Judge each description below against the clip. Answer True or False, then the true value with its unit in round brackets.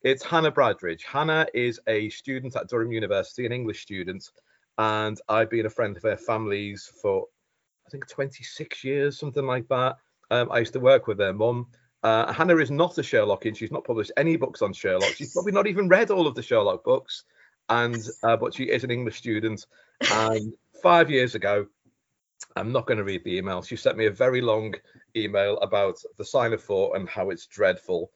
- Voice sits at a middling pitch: False (130 Hz)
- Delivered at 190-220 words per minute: True (200 wpm)